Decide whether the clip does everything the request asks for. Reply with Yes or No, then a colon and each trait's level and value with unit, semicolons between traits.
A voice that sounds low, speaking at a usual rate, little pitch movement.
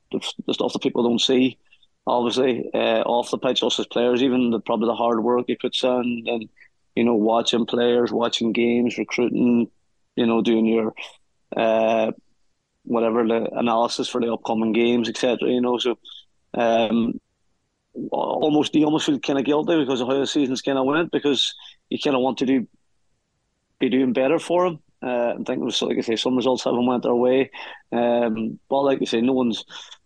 Yes: low, 120 Hz; average, 190 wpm; narrow, 2.2 semitones